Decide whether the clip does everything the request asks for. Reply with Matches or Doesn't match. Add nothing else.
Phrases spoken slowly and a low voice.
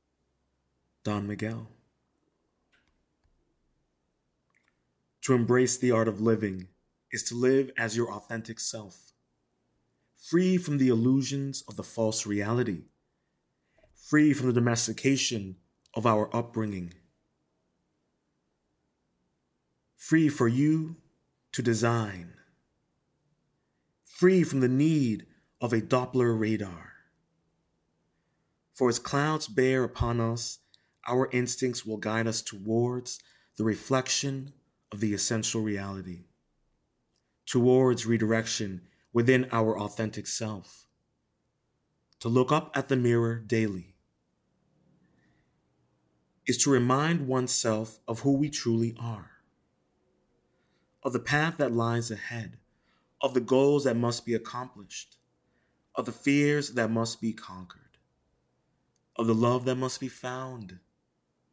Matches